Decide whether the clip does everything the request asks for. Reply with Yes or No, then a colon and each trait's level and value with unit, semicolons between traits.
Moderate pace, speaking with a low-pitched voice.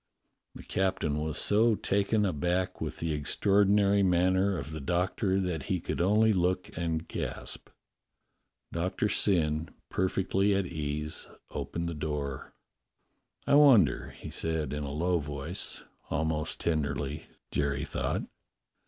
No: slow, 130 wpm; very low, 85 Hz